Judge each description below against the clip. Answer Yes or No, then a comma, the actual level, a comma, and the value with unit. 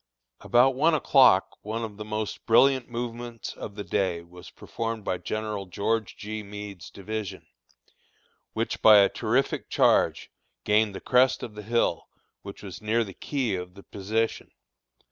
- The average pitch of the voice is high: No, low, 110 Hz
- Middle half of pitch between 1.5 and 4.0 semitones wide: Yes, average, 2.9 semitones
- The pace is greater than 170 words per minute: No, average, 155 wpm